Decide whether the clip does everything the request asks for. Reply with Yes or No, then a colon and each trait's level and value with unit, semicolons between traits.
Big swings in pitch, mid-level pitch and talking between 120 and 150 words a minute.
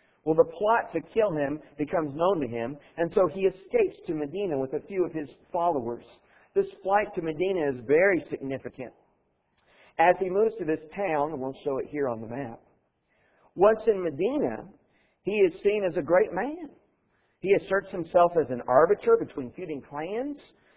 No: wide, 6.3 semitones; medium, 180 Hz; average, 175 wpm